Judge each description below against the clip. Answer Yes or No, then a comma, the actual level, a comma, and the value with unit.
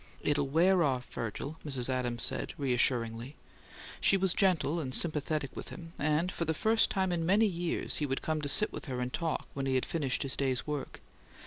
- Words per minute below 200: No, fast, 205 wpm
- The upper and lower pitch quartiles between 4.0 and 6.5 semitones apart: Yes, average, 4.4 semitones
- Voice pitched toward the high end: No, medium, 150 Hz